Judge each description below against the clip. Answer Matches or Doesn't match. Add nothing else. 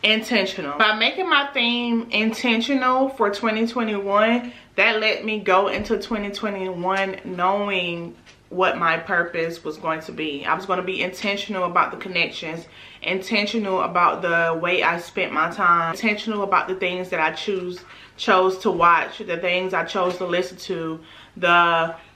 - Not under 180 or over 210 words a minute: Doesn't match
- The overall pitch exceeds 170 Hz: Matches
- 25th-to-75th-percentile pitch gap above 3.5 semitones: Matches